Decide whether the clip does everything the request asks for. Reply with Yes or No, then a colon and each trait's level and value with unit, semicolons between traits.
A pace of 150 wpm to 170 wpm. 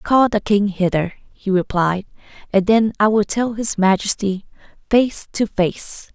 Yes: average, 155 wpm